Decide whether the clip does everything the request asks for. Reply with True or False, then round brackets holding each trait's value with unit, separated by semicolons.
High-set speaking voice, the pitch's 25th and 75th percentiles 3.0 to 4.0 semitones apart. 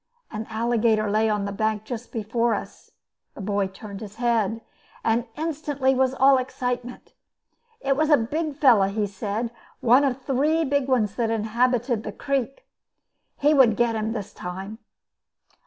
True (235 Hz; 3.6 semitones)